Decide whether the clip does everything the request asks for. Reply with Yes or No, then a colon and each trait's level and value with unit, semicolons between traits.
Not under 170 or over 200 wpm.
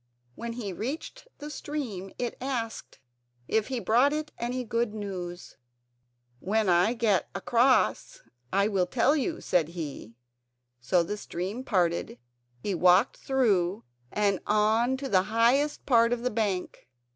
No: average, 140 wpm